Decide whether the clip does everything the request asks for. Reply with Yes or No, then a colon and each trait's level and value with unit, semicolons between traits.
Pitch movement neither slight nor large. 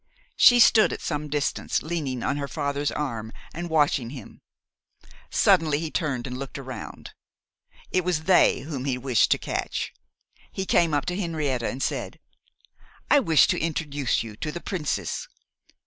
Yes: average, 3.9 semitones